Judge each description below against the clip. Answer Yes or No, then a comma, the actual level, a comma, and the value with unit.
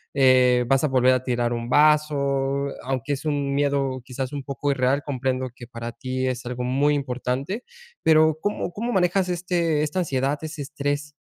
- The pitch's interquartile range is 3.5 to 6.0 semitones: No, average, 2.7 semitones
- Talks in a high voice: No, medium, 140 Hz